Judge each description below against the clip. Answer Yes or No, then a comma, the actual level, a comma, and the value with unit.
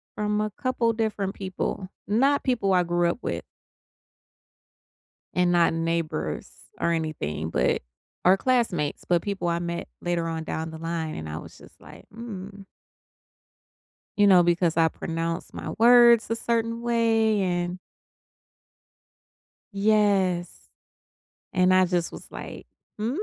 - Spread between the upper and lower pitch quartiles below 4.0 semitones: No, average, 4.4 semitones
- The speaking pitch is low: No, medium, 185 Hz